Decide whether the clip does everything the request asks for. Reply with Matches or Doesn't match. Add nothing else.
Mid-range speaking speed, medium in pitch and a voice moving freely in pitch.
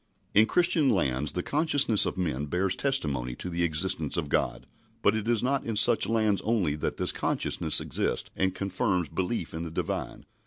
Doesn't match